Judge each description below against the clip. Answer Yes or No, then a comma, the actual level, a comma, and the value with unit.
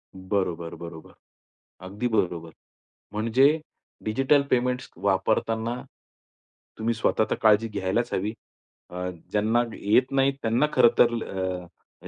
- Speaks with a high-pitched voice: No, low, 110 Hz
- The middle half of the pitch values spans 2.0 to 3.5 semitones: No, average, 4.0 semitones